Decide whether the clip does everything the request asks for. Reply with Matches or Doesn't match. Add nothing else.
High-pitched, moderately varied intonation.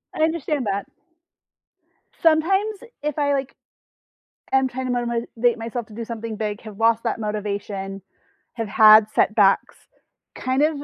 Matches